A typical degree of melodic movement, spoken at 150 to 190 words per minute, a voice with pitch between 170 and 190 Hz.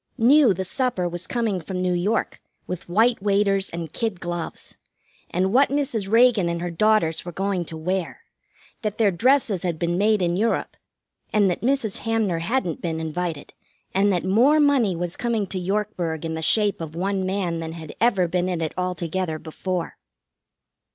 Yes: average, 4.1 semitones; average, 180 wpm; medium, 185 Hz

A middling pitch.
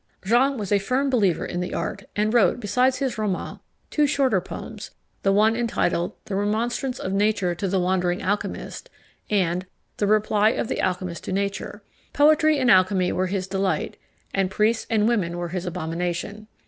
No: high, 205 Hz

